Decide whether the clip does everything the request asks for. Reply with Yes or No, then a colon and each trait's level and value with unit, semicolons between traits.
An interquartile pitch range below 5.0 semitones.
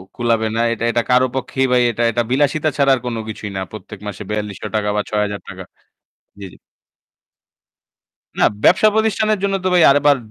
No: wide, 5.4 semitones